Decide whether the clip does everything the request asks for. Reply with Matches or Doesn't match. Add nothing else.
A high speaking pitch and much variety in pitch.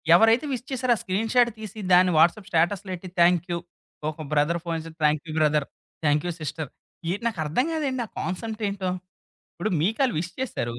Doesn't match